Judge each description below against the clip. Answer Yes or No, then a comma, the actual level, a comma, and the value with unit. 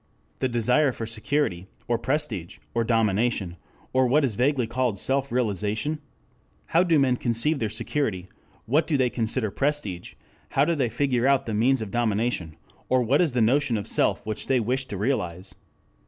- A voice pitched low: Yes, low, 120 Hz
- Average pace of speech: Yes, average, 175 wpm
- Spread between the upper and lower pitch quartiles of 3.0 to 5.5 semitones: Yes, average, 4.0 semitones